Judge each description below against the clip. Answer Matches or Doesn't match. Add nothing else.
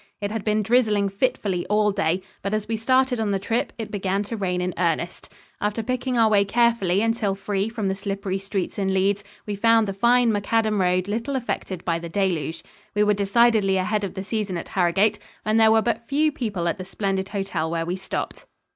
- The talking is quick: Matches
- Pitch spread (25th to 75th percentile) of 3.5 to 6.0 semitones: Doesn't match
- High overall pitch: Matches